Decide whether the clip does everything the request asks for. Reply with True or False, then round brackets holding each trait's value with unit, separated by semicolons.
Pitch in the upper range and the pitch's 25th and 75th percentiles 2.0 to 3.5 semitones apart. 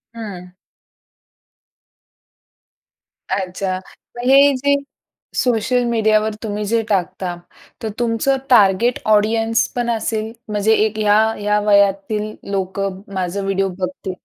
True (210 Hz; 2.8 semitones)